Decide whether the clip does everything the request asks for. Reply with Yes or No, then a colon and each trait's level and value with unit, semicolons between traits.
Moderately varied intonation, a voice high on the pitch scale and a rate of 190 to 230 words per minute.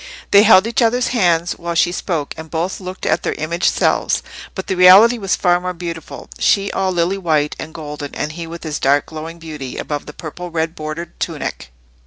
No: average, 3.0 semitones; medium, 170 Hz; fast, 205 wpm